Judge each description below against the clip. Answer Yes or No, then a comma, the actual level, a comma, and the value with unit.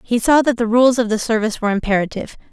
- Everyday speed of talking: No, fast, 240 wpm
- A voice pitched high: Yes, high, 230 Hz